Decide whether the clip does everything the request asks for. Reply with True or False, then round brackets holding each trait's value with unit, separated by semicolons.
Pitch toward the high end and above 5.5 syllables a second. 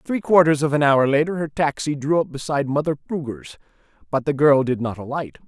False (145 Hz; 5.8 syllables/s)